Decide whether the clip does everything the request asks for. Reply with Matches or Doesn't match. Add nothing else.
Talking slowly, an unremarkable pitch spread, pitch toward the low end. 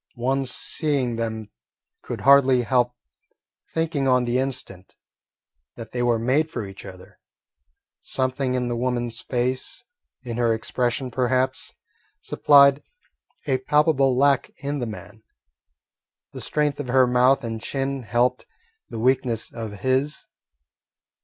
Doesn't match